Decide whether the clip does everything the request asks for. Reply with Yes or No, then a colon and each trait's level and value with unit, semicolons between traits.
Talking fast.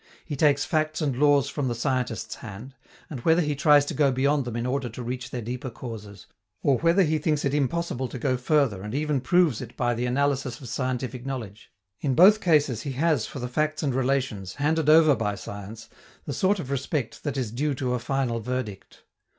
Yes: fast, 210 wpm